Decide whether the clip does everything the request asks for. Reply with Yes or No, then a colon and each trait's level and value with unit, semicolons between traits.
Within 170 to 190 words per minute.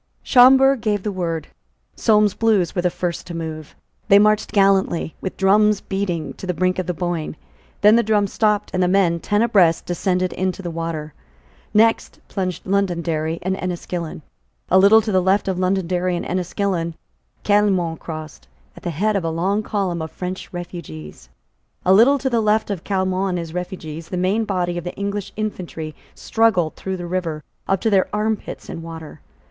Yes: average, 180 wpm